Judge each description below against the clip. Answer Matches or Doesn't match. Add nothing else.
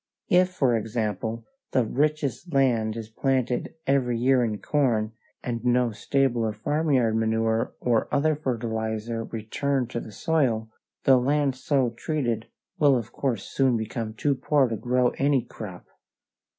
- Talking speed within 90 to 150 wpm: Matches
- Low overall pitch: Matches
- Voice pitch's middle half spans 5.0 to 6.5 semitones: Doesn't match